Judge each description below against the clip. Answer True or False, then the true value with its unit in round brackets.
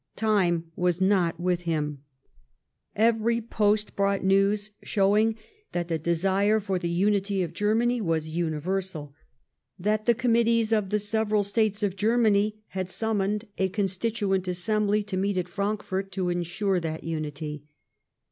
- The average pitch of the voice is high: True (195 Hz)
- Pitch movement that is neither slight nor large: True (3.3 semitones)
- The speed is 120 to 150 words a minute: True (140 wpm)